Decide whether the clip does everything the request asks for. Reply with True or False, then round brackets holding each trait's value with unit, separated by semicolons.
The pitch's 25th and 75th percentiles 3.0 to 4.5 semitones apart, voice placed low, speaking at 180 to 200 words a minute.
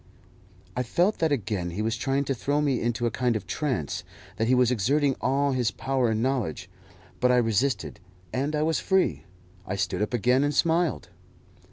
True (4.0 semitones; 125 Hz; 190 wpm)